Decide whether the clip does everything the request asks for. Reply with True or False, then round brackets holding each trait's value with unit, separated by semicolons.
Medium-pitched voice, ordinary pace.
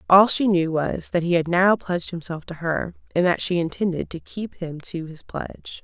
False (175 Hz; 225 wpm)